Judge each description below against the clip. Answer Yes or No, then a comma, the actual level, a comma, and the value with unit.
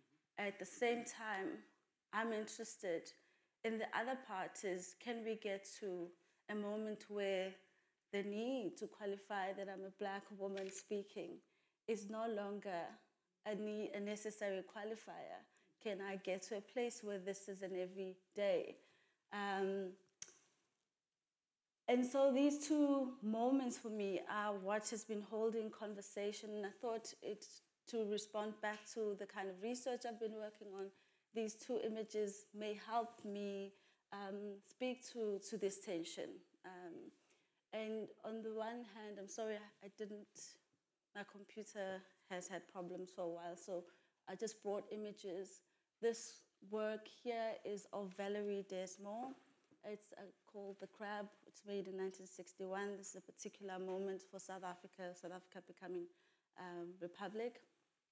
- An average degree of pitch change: No, narrow, 2.3 semitones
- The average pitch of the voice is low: No, high, 205 Hz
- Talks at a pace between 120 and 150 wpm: Yes, average, 145 wpm